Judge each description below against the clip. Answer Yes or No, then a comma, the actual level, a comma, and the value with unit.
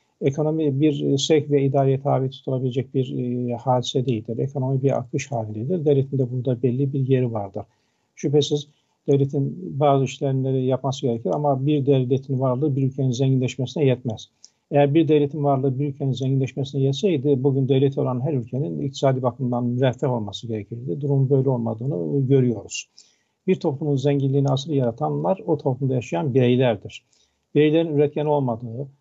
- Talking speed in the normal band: No, fast, 145 wpm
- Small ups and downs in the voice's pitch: Yes, narrow, 2.0 semitones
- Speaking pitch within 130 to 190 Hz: Yes, low, 135 Hz